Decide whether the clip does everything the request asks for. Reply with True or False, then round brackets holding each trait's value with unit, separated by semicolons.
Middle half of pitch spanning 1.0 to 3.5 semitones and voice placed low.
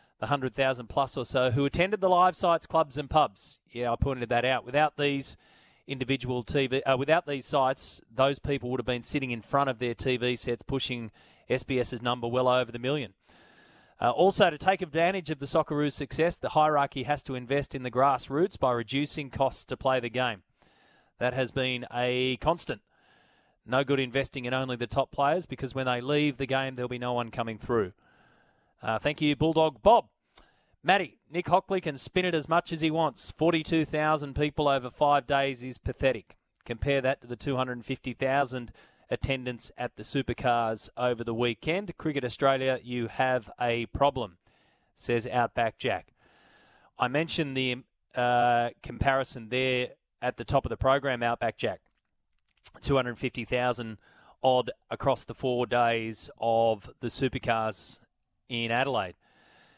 True (2.9 semitones; 130 Hz)